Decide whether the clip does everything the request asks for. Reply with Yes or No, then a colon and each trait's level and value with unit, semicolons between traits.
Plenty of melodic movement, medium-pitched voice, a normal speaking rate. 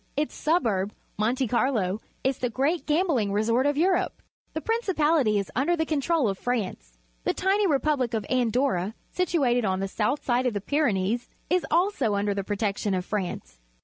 No: wide, 6.8 semitones; high, 245 Hz; average, 170 wpm